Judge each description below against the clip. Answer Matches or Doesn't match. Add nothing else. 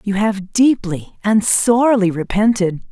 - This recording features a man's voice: Doesn't match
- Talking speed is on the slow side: Matches